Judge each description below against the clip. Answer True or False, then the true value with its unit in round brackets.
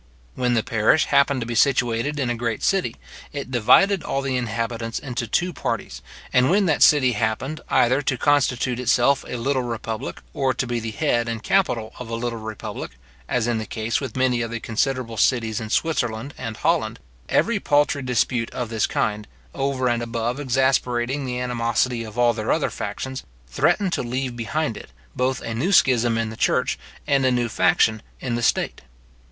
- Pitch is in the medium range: False (120 Hz)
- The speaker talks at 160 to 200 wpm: True (190 wpm)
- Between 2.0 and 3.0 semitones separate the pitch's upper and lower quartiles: True (2.7 semitones)